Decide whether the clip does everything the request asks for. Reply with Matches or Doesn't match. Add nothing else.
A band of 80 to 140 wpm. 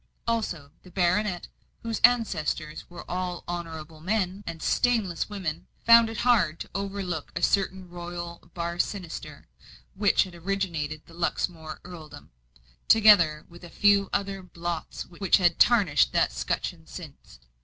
Matches